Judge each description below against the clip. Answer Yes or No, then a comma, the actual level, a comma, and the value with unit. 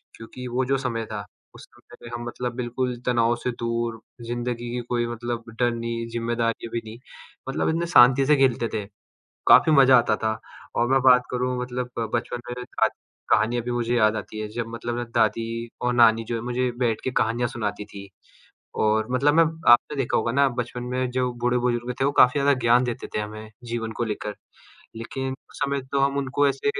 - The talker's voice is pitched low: Yes, low, 120 Hz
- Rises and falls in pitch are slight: Yes, narrow, 1.5 semitones